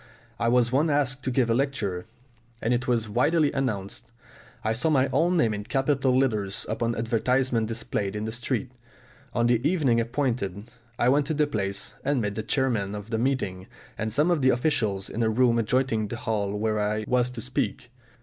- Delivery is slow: No, average, 195 wpm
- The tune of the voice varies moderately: Yes, average, 3.5 semitones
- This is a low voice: Yes, low, 120 Hz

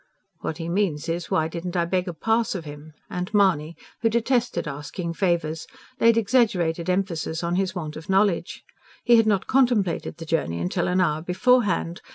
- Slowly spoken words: No, average, 180 wpm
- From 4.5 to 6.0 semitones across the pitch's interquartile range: No, average, 4.0 semitones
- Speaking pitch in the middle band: Yes, medium, 180 Hz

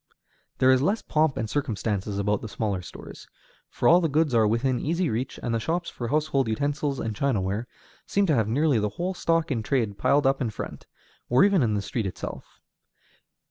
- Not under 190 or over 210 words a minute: Yes, average, 200 wpm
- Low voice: Yes, low, 130 Hz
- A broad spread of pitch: Yes, wide, 5.7 semitones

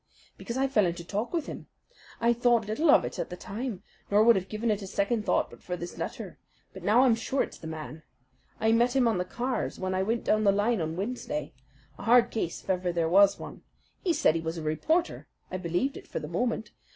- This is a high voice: Yes, high, 210 Hz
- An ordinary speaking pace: No, fast, 240 wpm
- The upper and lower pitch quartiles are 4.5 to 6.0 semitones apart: Yes, average, 5.1 semitones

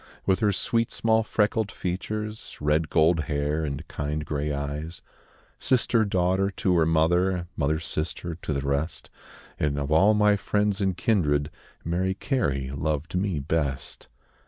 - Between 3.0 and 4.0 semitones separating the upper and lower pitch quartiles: No, average, 5.0 semitones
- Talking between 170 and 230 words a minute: No, average, 145 wpm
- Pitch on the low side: Yes, very low, 85 Hz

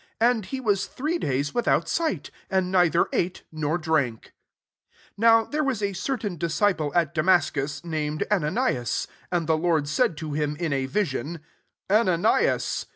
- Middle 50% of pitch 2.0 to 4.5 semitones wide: No, wide, 5.4 semitones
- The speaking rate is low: No, average, 165 wpm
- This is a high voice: No, medium, 170 Hz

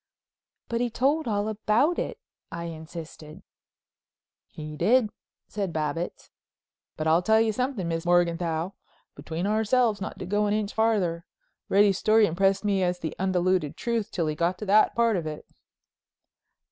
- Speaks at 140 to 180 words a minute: Yes, average, 145 wpm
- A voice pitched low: No, high, 195 Hz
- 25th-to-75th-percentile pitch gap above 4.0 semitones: Yes, average, 4.5 semitones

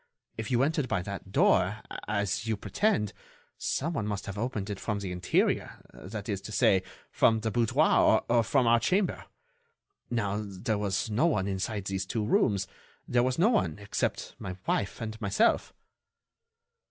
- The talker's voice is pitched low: Yes, low, 105 Hz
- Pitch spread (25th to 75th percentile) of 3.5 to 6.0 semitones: No, average, 3.1 semitones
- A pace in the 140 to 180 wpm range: Yes, average, 165 wpm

